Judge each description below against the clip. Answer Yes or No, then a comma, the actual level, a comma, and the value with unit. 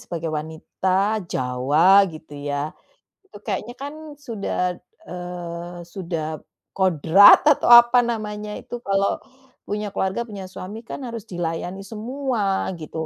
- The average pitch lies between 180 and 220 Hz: Yes, high, 190 Hz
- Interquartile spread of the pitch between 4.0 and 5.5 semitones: Yes, average, 4.4 semitones